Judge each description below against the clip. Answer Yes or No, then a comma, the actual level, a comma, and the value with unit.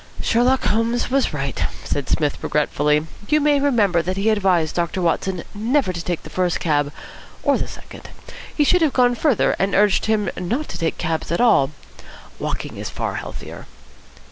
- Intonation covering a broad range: Yes, wide, 6.6 semitones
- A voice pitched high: Yes, high, 195 Hz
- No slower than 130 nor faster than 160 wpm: No, average, 175 wpm